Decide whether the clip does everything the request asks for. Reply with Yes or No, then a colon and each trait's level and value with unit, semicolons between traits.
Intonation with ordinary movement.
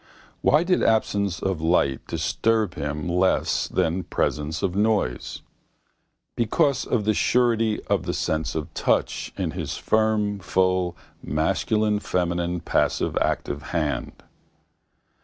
Yes: average, 4.9 semitones